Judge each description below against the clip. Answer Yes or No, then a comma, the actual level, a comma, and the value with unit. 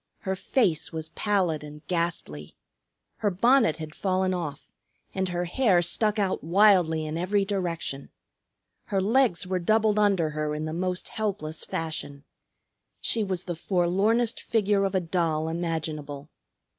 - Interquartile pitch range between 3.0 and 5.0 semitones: Yes, average, 4.0 semitones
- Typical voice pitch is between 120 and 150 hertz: No, medium, 180 Hz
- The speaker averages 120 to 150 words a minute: Yes, average, 145 wpm